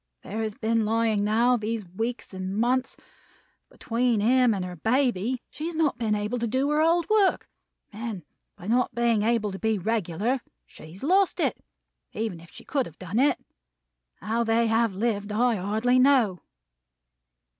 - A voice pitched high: Yes, high, 225 Hz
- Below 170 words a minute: No, average, 175 wpm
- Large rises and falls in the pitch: No, average, 3.2 semitones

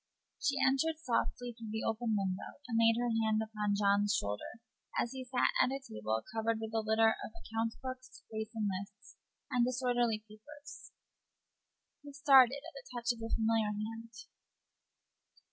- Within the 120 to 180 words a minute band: Yes, average, 160 wpm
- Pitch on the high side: Yes, high, 225 Hz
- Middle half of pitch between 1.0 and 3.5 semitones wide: Yes, average, 2.9 semitones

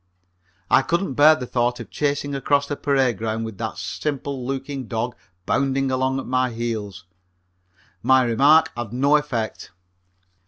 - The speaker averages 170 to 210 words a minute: No, average, 150 wpm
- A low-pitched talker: Yes, low, 130 Hz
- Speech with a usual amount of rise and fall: Yes, average, 3.4 semitones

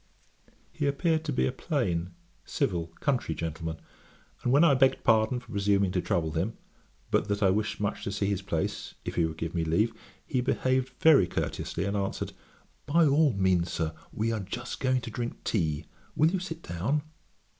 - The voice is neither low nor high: No, low, 105 Hz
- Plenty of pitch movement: Yes, wide, 7.1 semitones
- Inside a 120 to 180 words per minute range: No, average, 190 wpm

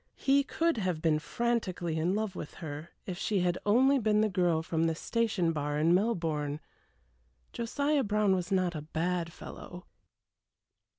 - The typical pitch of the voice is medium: Yes, medium, 180 Hz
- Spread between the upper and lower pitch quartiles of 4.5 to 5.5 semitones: Yes, average, 5.0 semitones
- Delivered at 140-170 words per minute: Yes, average, 160 wpm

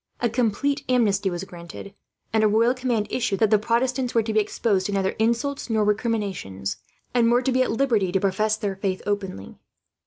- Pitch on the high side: Yes, high, 215 Hz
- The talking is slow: No, average, 195 wpm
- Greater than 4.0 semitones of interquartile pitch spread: No, average, 3.4 semitones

